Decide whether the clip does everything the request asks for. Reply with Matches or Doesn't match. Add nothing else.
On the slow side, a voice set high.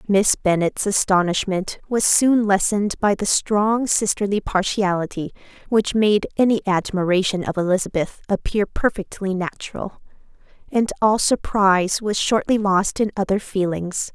Matches